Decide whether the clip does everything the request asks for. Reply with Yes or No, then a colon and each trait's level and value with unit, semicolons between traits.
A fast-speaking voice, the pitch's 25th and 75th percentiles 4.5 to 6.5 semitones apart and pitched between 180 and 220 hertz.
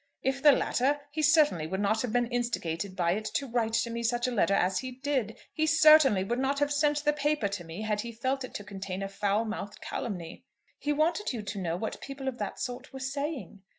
No: fast, 235 wpm; wide, 5.6 semitones; high, 240 Hz